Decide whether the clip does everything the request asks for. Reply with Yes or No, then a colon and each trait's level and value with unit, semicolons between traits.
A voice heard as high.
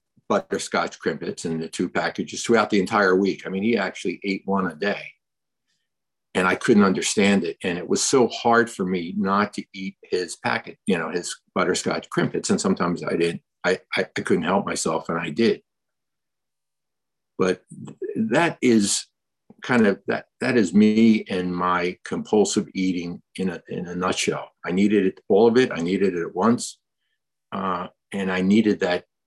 No: very low, 95 Hz